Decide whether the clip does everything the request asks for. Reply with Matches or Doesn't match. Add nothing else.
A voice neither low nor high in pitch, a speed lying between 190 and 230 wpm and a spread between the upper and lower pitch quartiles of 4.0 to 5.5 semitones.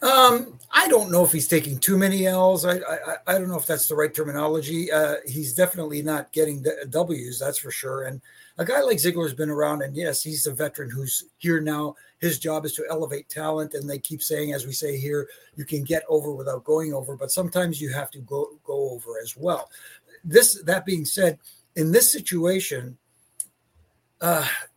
Doesn't match